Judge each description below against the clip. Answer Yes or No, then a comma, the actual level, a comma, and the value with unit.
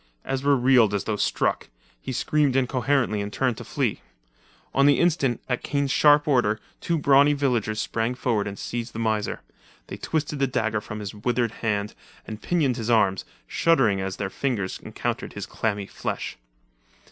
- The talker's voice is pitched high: No, low, 120 Hz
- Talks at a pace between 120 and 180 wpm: Yes, average, 170 wpm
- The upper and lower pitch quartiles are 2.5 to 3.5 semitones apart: No, average, 4.5 semitones